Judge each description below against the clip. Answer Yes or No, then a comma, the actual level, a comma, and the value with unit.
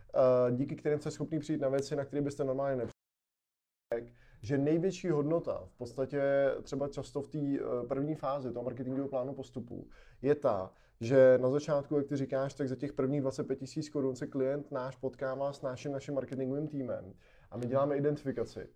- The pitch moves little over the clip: Yes, narrow, 1.9 semitones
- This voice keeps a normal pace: No, fast, 175 wpm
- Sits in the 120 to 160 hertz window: Yes, low, 135 Hz